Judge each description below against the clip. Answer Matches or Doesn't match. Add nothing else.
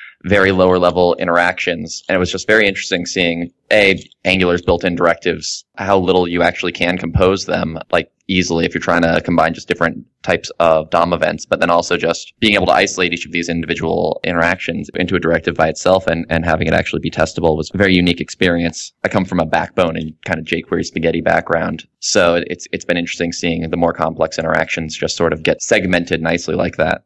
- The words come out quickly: Matches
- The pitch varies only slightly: Matches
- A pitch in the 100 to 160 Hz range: Doesn't match